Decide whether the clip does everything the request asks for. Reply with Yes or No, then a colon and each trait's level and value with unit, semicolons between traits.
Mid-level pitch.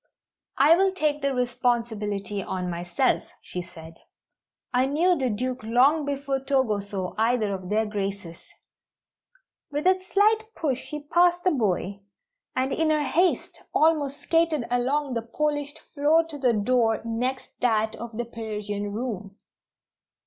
No: very high, 250 Hz